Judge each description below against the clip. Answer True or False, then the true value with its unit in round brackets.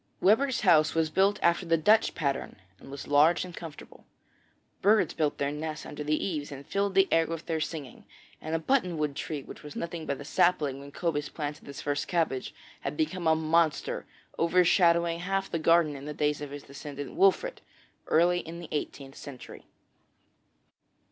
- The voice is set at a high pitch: False (160 Hz)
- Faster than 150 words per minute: True (180 wpm)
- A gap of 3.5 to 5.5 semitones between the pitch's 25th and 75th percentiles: False (3.1 semitones)